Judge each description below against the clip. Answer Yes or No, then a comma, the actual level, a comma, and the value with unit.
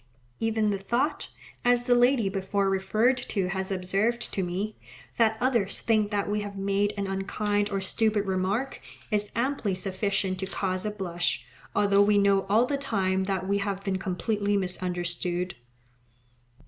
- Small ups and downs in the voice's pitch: Yes, narrow, 2.2 semitones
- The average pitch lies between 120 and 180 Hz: No, high, 200 Hz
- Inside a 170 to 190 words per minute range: No, average, 160 wpm